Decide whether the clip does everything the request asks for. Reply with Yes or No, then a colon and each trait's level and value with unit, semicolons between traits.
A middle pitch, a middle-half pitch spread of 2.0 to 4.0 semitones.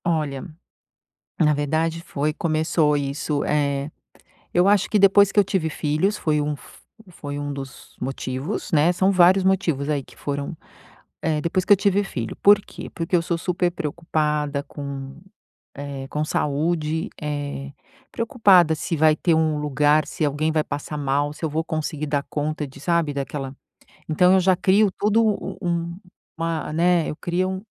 Yes: medium, 155 Hz; average, 3.5 semitones